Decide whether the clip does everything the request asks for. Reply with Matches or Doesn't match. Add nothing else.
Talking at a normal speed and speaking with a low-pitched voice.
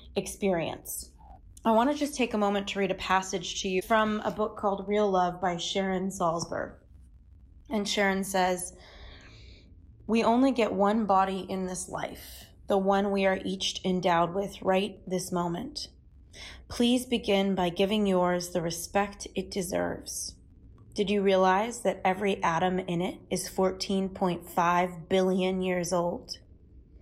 Doesn't match